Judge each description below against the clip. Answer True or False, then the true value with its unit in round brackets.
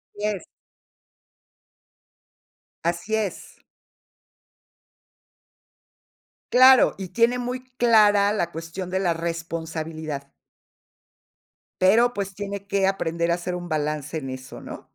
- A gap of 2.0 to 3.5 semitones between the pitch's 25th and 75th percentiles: False (4.0 semitones)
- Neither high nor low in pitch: True (180 Hz)